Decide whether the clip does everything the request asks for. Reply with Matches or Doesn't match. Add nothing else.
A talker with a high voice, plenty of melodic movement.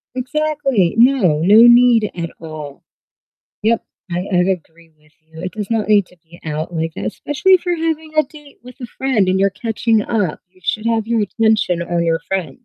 Matches